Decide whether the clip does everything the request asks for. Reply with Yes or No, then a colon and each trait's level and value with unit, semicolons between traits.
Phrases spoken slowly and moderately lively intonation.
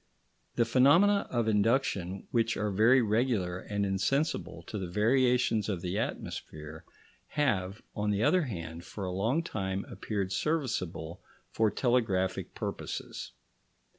Yes: slow, 130 wpm; average, 4.9 semitones